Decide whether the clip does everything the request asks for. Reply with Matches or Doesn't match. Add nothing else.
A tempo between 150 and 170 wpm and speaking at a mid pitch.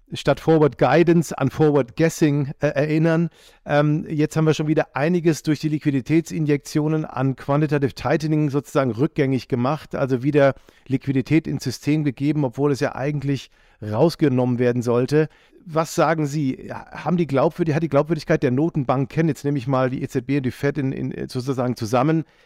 Matches